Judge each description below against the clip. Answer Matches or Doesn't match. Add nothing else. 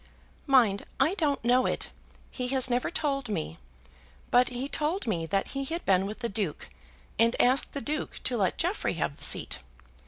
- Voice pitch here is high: Matches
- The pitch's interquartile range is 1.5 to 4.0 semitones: Doesn't match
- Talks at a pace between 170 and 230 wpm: Matches